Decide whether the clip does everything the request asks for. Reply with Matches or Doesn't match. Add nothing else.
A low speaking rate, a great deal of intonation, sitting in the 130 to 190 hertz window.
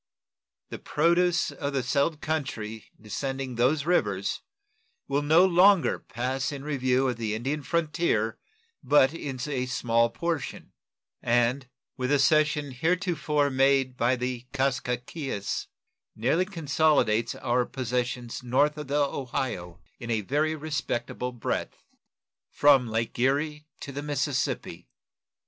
Doesn't match